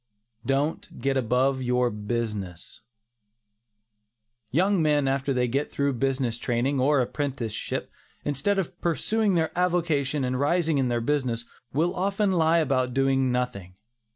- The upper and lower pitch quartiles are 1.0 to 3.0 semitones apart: No, average, 4.3 semitones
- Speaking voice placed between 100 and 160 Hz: Yes, low, 135 Hz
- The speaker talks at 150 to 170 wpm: No, slow, 135 wpm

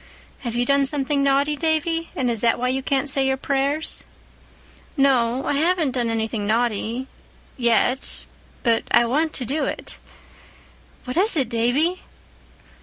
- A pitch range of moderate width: Yes, average, 3.5 semitones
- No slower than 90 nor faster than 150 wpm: Yes, average, 145 wpm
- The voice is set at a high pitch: Yes, very high, 265 Hz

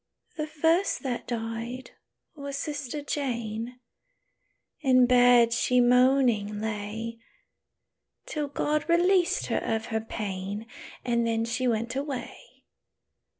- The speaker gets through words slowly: Yes, slow, 110 wpm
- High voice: Yes, high, 245 Hz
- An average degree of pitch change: Yes, average, 3.7 semitones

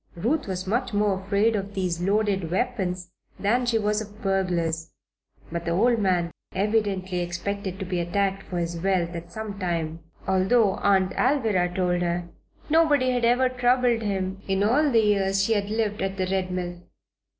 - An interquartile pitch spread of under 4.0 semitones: Yes, average, 3.4 semitones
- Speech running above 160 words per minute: Yes, average, 170 wpm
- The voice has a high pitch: Yes, high, 195 Hz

